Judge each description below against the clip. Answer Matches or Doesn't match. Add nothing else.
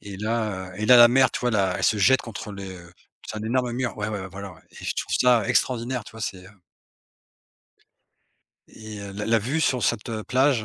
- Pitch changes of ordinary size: Matches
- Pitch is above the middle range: Doesn't match